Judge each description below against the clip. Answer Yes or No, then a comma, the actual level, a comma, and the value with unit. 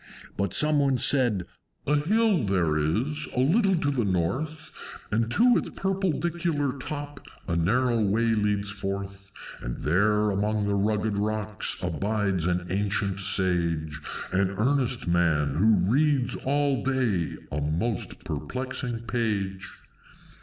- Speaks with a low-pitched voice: Yes, low, 105 Hz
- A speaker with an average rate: No, slow, 130 wpm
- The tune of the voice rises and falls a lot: Yes, wide, 6.1 semitones